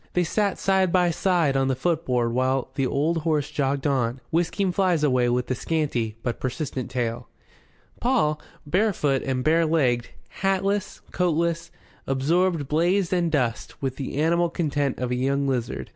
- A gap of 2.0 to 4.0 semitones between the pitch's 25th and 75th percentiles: No, average, 4.8 semitones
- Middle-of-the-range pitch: Yes, medium, 150 Hz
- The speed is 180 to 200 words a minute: No, average, 155 wpm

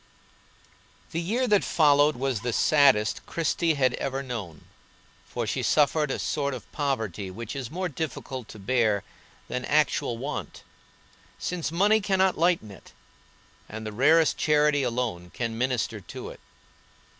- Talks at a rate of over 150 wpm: No, average, 145 wpm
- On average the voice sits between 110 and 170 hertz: Yes, low, 135 Hz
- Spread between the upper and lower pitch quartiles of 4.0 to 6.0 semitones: Yes, wide, 5.5 semitones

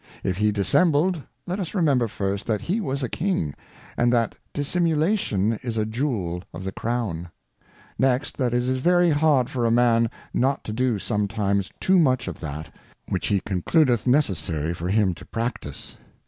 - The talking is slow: No, average, 175 wpm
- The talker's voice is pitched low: Yes, low, 120 Hz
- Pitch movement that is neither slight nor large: No, wide, 6.4 semitones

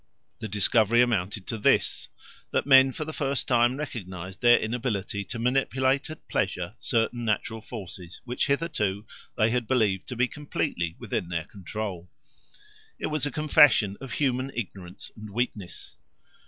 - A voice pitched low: Yes, low, 115 Hz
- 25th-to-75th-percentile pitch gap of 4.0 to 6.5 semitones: Yes, average, 4.9 semitones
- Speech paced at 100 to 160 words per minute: Yes, average, 150 wpm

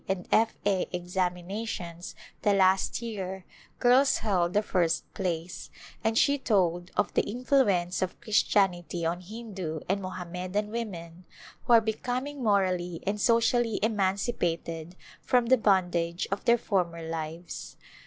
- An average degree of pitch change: Yes, average, 4.1 semitones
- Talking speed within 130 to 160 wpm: Yes, slow, 135 wpm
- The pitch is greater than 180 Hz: Yes, high, 190 Hz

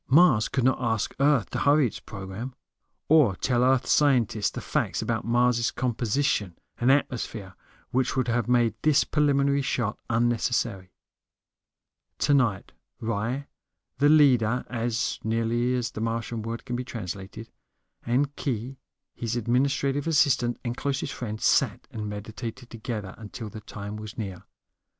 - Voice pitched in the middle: No, low, 120 Hz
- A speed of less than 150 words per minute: Yes, average, 140 wpm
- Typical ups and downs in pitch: Yes, average, 3.3 semitones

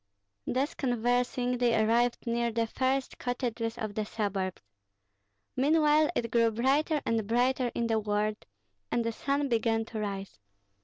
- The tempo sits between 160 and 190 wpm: No, average, 145 wpm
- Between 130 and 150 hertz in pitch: No, high, 235 Hz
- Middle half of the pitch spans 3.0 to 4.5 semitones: No, narrow, 2.4 semitones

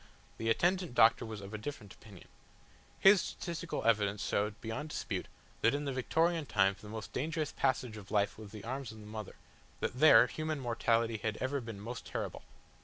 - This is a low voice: Yes, low, 115 Hz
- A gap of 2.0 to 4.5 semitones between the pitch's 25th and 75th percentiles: No, average, 5.0 semitones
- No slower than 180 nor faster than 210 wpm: Yes, average, 185 wpm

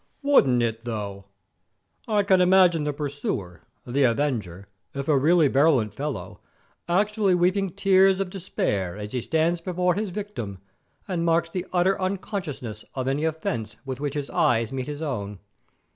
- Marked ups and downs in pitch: Yes, wide, 7.3 semitones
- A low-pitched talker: No, medium, 150 Hz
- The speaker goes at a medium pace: Yes, average, 155 wpm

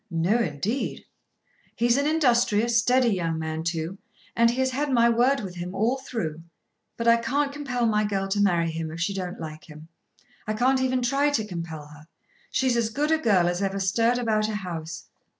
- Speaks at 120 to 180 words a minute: No, average, 200 wpm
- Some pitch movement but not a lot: No, wide, 6.2 semitones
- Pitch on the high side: Yes, high, 215 Hz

